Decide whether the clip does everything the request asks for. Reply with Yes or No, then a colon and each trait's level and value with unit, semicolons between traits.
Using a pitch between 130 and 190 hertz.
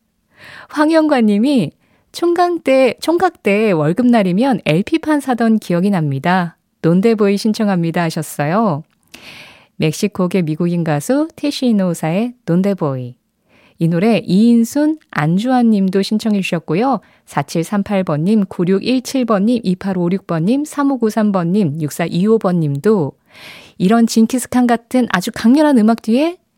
No: high, 210 Hz